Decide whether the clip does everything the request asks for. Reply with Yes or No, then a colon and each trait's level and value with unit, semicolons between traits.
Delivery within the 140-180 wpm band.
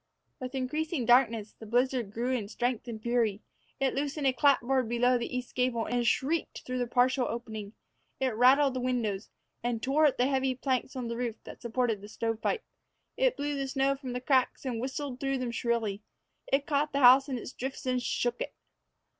No: average, 195 wpm